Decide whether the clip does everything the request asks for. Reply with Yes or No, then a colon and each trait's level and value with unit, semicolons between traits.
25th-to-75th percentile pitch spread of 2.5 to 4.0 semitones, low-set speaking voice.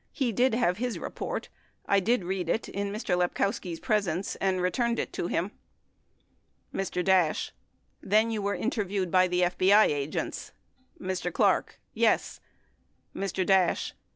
No: average, 2.9 semitones; high, 190 Hz